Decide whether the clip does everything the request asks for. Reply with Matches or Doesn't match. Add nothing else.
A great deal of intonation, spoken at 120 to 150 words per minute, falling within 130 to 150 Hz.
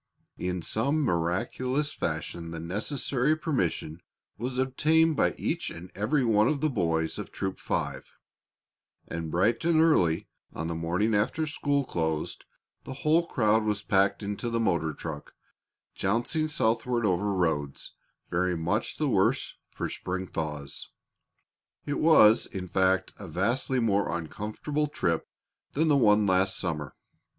Doesn't match